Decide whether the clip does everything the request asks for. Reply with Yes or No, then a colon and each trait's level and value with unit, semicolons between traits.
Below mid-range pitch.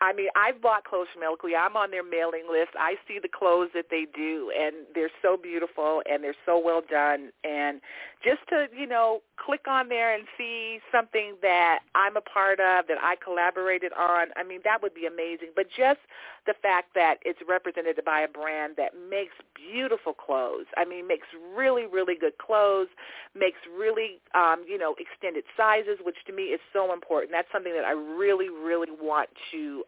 No: medium, 185 Hz